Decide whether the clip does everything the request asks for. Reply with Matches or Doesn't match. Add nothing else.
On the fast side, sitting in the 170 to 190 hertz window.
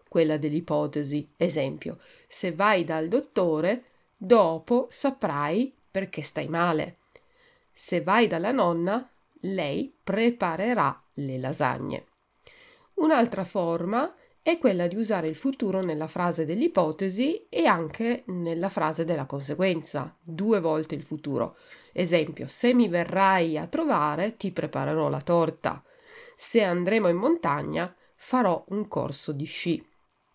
Doesn't match